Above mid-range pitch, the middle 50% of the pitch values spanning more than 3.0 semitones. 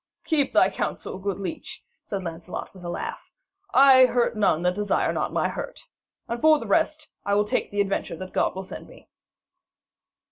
Yes: high, 205 Hz; wide, 5.6 semitones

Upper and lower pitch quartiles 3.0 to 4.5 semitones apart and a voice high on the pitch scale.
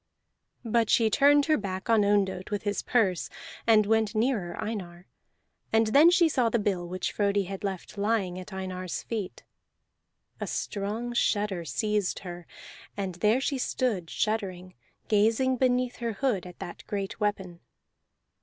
Yes: average, 3.5 semitones; high, 205 Hz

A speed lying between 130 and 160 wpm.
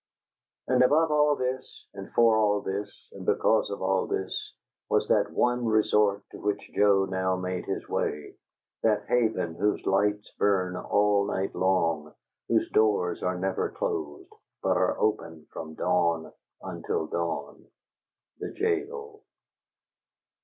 Yes: slow, 135 wpm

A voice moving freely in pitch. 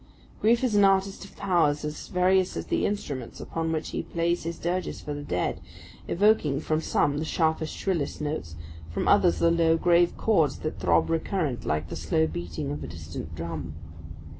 Yes: wide, 5.9 semitones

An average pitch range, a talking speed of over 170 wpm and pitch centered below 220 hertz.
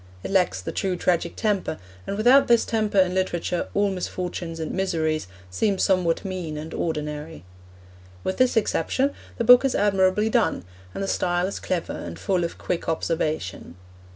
No: average, 3.8 semitones; average, 165 wpm; medium, 185 Hz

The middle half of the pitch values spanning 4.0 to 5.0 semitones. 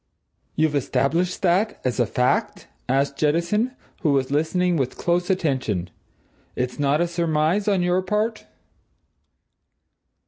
Yes: average, 4.7 semitones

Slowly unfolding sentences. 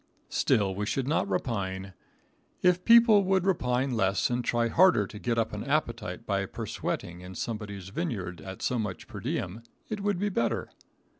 No: average, 170 wpm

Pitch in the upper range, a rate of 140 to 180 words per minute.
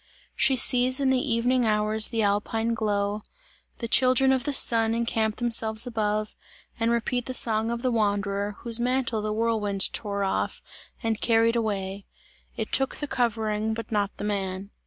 Yes: high, 225 Hz; average, 165 wpm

